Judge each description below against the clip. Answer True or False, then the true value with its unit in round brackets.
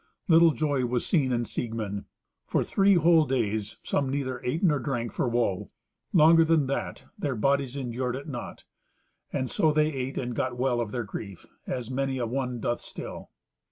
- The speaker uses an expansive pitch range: False (3.3 semitones)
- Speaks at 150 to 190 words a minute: True (180 wpm)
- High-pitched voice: False (130 Hz)